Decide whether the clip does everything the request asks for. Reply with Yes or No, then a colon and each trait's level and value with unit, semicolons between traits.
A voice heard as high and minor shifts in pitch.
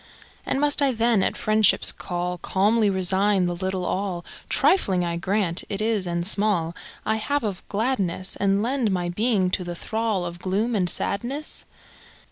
No: high, 195 Hz; average, 3.5 semitones